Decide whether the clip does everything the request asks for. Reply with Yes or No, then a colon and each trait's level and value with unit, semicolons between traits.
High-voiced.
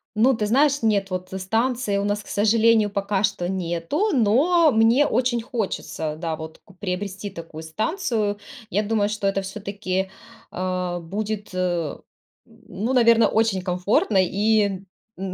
Yes: high, 205 Hz